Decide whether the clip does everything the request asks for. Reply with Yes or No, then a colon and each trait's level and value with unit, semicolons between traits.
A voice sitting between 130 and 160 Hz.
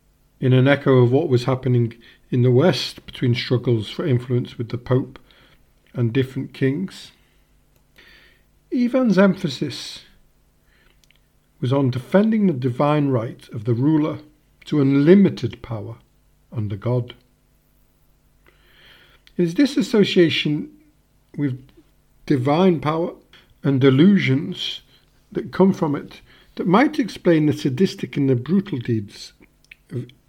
Yes: medium, 140 Hz